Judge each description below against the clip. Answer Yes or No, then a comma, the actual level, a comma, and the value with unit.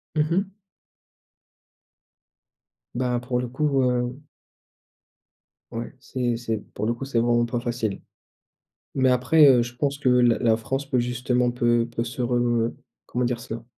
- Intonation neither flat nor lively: No, narrow, 1.3 semitones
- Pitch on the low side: Yes, low, 125 Hz